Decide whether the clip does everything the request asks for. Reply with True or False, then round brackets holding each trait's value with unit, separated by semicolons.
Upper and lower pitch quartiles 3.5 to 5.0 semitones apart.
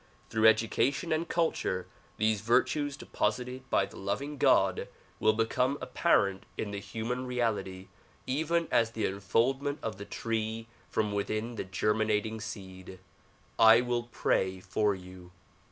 True (3.8 semitones)